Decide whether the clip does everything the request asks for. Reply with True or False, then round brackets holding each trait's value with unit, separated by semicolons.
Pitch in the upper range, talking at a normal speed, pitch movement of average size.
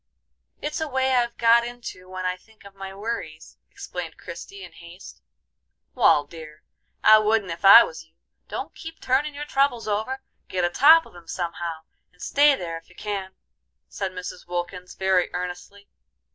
False (200 Hz; 170 wpm; 6.0 semitones)